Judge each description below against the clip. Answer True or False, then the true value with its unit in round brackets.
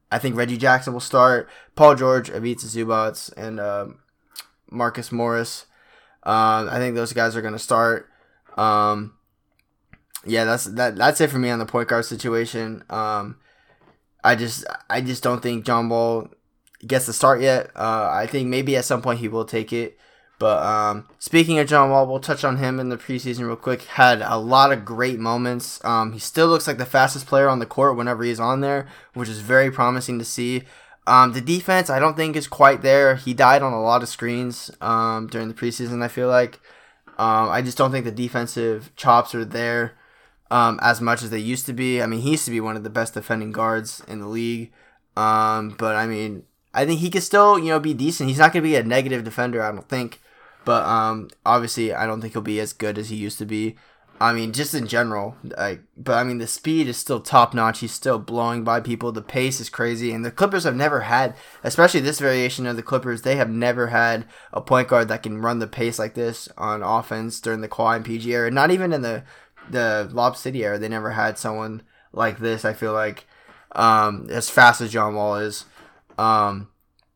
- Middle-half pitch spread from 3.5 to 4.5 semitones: False (2.4 semitones)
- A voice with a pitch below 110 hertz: False (120 Hz)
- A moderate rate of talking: False (220 wpm)